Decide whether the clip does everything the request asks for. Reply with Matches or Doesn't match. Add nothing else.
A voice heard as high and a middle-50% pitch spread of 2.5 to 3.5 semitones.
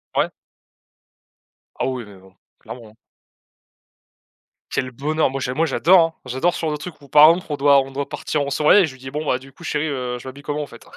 Doesn't match